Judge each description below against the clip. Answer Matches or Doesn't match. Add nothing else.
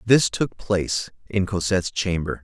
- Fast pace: Doesn't match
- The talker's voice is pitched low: Matches